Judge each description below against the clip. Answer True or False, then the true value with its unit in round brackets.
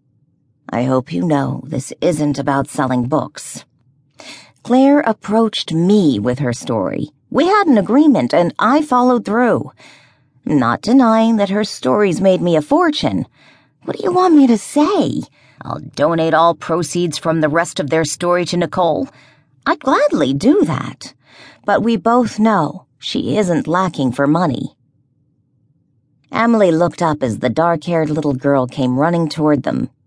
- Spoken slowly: False (155 wpm)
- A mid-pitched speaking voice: True (170 Hz)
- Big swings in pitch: True (7.9 semitones)